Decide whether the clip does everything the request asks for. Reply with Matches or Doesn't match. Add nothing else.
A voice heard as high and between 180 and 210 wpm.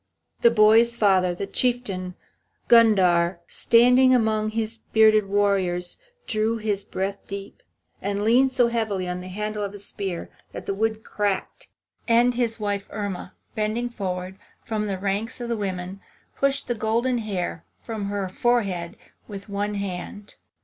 Doesn't match